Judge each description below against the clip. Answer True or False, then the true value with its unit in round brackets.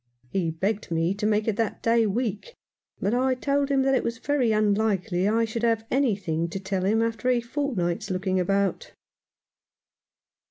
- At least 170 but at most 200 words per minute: True (175 wpm)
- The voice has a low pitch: False (215 Hz)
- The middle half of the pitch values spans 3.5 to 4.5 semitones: True (3.9 semitones)